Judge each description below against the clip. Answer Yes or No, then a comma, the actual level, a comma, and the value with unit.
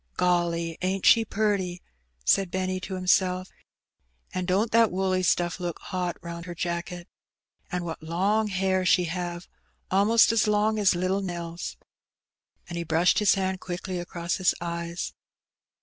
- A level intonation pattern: Yes, narrow, 1.9 semitones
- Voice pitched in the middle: Yes, medium, 180 Hz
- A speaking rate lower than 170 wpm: Yes, average, 160 wpm